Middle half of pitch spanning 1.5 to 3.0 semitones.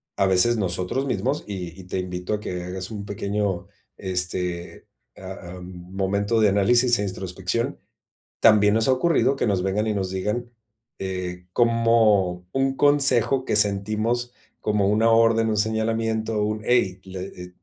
No: average, 3.5 semitones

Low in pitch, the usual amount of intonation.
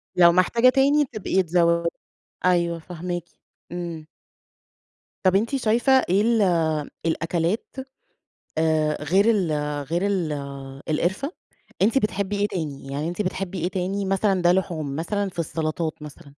No: medium, 180 Hz; average, 3.4 semitones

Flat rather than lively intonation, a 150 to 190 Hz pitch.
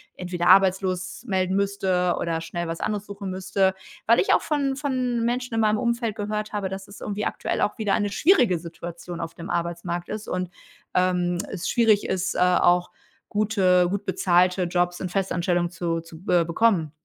No: average, 3.0 semitones; medium, 185 Hz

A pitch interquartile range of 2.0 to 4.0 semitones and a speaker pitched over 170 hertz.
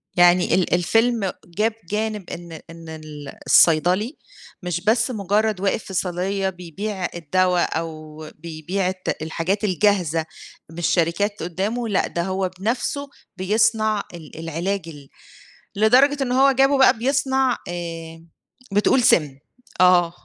No: average, 4.4 semitones; medium, 185 Hz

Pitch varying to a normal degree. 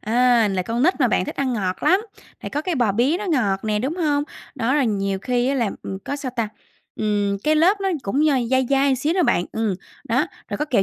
No: wide, 5.7 semitones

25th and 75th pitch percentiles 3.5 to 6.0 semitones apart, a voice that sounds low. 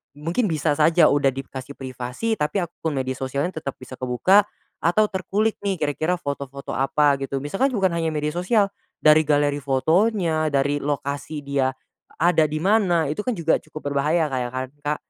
No: average, 4.0 semitones; medium, 150 Hz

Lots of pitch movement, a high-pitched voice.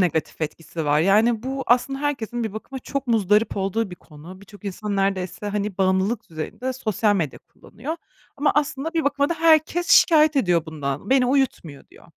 Yes: wide, 6.6 semitones; high, 215 Hz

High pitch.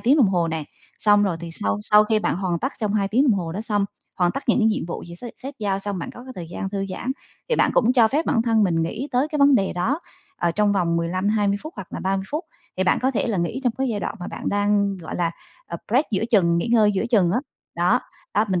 Yes: high, 205 Hz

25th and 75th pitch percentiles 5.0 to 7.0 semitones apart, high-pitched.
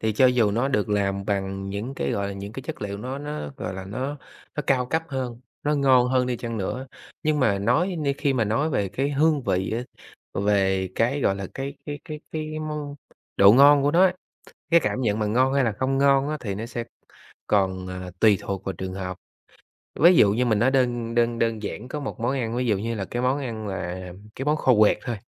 No: average, 5.3 semitones; low, 120 Hz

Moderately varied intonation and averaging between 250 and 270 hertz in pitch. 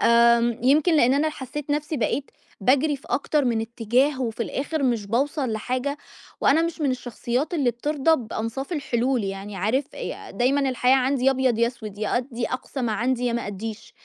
Yes: average, 3.3 semitones; very high, 255 Hz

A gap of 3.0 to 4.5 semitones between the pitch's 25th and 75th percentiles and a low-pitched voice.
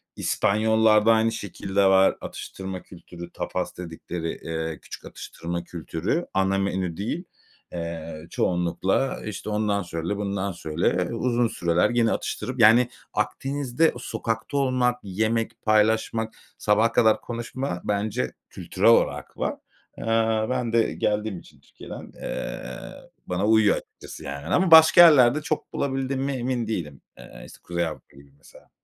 No: average, 5.1 semitones; low, 110 Hz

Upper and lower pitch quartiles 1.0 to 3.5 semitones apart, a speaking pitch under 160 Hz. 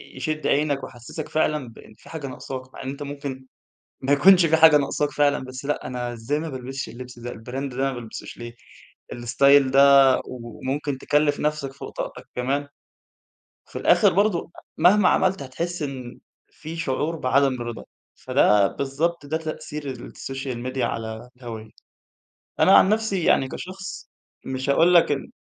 Yes: average, 3.2 semitones; medium, 140 Hz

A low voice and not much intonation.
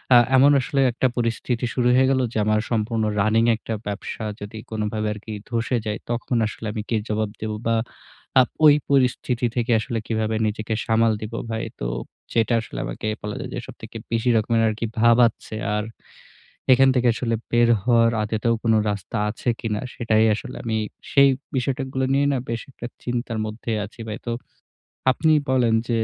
Yes: low, 115 Hz; narrow, 2.2 semitones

